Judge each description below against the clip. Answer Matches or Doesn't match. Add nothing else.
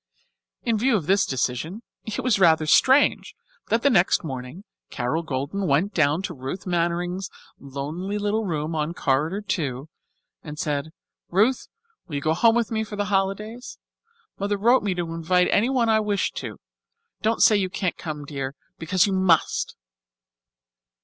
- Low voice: Doesn't match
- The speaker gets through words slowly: Doesn't match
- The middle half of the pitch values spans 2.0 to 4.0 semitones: Doesn't match